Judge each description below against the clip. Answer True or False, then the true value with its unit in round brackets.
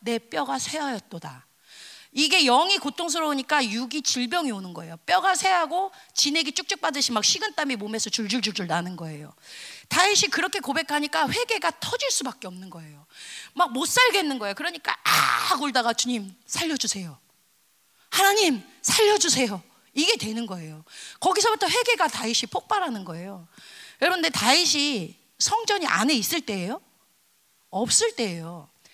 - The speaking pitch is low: False (275 Hz)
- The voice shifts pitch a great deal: True (9.0 semitones)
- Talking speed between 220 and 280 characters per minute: False (335 characters per minute)